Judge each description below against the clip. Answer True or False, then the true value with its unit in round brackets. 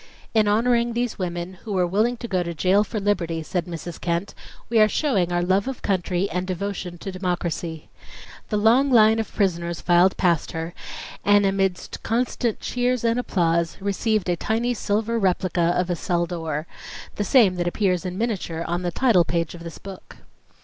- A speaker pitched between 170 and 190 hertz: True (185 Hz)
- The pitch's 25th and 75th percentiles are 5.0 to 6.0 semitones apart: False (3.9 semitones)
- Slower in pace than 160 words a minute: False (185 wpm)